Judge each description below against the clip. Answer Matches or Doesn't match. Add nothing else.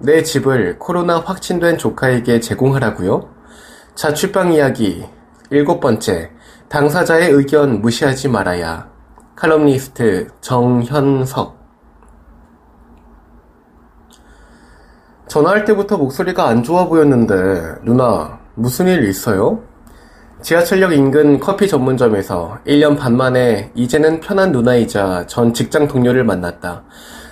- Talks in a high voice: Doesn't match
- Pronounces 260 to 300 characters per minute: Doesn't match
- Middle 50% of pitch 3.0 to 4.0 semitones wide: Doesn't match